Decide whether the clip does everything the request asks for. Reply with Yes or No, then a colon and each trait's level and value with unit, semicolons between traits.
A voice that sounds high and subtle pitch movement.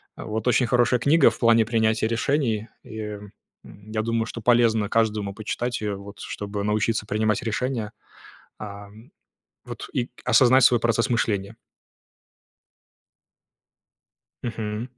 No: low, 110 Hz; narrow, 2.2 semitones